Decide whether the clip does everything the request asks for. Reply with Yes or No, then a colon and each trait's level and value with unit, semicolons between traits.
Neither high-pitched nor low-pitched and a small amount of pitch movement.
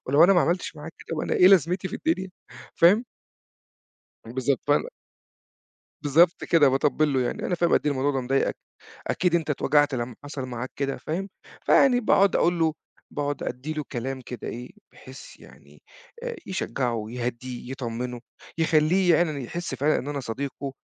No: medium, 145 Hz; average, 4.8 semitones